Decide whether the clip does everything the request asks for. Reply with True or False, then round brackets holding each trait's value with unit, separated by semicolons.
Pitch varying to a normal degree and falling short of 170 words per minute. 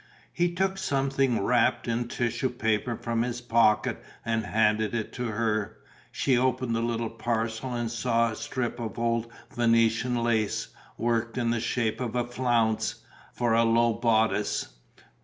False (1.4 semitones; 155 wpm)